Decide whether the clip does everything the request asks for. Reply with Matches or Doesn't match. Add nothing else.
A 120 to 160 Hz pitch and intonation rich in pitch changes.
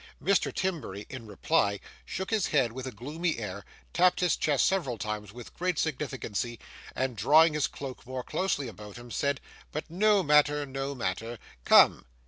Matches